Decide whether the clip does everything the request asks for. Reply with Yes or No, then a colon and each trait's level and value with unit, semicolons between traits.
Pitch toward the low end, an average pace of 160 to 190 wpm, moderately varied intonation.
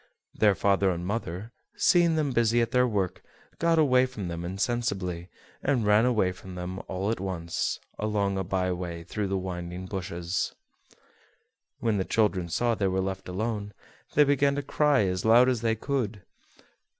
Yes: low, 100 Hz; average, 170 wpm; average, 4.5 semitones